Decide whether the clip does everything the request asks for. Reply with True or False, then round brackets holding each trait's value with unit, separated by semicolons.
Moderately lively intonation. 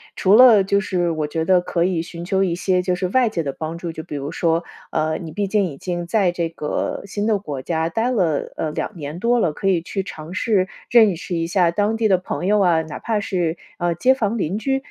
True (3.6 semitones)